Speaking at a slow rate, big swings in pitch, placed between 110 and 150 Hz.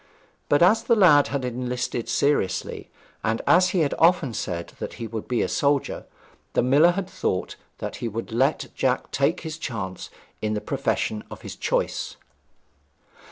No: average, 165 wpm; wide, 6.2 semitones; low, 135 Hz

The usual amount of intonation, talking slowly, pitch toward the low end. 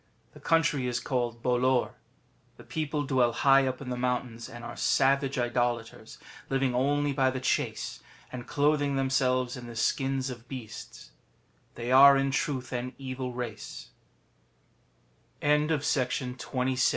No: narrow, 2.0 semitones; slow, 130 wpm; low, 130 Hz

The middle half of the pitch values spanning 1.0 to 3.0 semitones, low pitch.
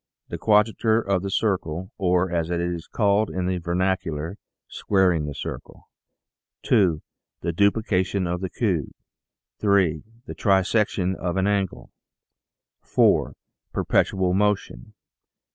Yes: narrow, 2.6 semitones; very low, 95 Hz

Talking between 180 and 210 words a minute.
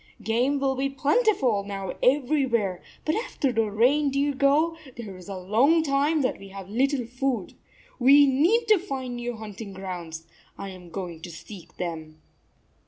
No: average, 160 wpm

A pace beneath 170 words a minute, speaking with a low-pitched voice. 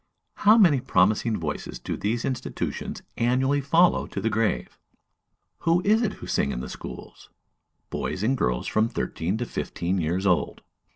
Yes: average, 160 wpm; low, 115 Hz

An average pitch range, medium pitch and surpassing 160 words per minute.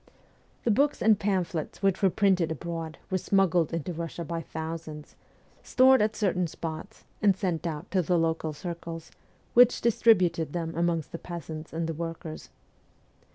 No: average, 3.0 semitones; medium, 170 Hz; average, 155 wpm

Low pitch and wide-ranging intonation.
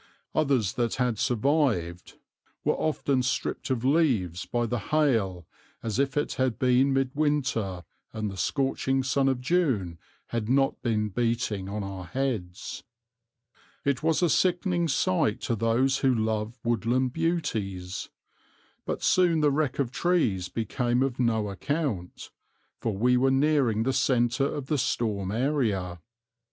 No: low, 125 Hz; average, 4.6 semitones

